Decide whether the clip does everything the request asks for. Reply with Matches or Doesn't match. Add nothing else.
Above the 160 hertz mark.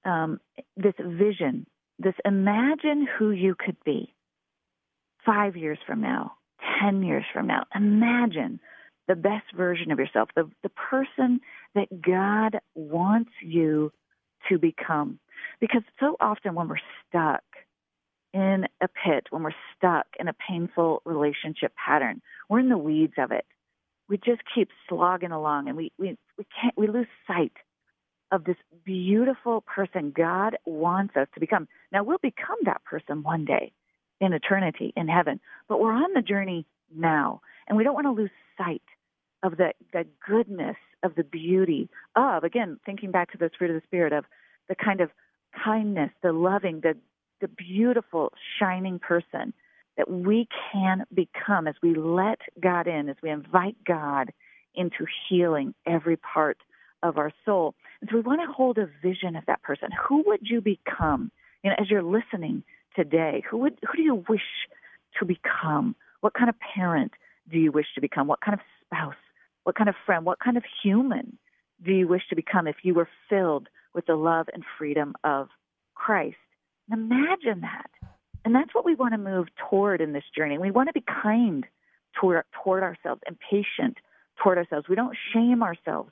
Matches